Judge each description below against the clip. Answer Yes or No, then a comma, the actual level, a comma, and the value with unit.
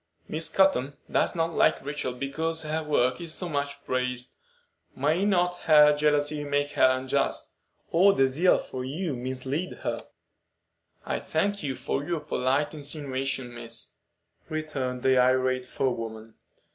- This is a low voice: No, medium, 145 Hz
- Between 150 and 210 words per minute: No, average, 140 wpm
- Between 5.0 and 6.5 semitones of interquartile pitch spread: No, average, 3.3 semitones